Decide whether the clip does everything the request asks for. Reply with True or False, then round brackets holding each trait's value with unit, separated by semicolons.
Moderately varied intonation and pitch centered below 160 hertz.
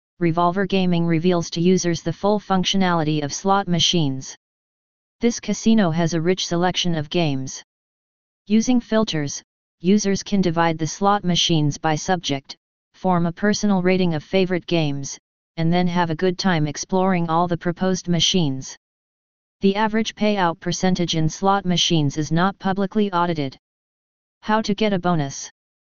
False (3.0 semitones; 175 Hz)